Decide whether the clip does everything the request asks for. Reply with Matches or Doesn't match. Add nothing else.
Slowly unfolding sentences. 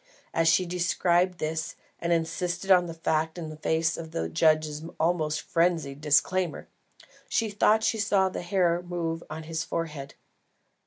Doesn't match